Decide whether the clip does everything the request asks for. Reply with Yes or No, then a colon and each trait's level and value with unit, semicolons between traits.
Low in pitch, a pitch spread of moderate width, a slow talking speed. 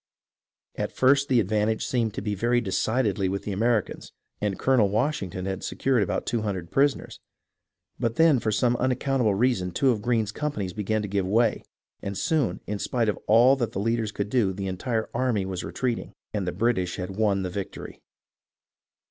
No: low, 110 Hz; average, 3.9 semitones; average, 180 wpm